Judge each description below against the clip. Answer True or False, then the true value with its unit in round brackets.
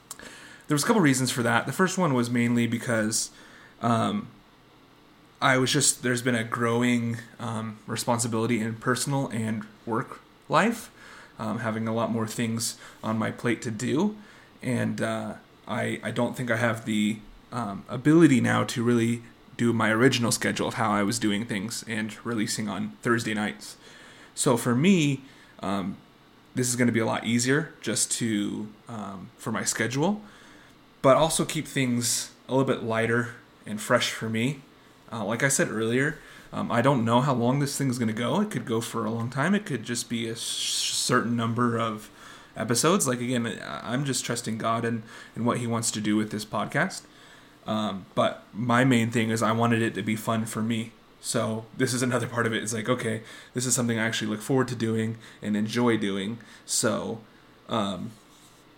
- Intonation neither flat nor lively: False (2.0 semitones)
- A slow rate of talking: False (190 wpm)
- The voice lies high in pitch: False (115 Hz)